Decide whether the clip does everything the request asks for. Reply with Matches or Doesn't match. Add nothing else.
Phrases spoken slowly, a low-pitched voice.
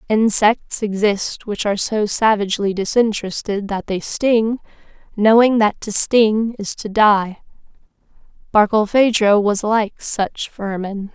Doesn't match